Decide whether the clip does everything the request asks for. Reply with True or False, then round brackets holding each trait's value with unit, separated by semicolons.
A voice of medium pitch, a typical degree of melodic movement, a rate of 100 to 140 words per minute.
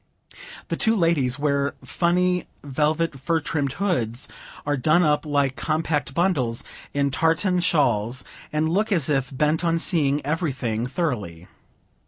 True (150 Hz; 3.8 semitones; 135 wpm)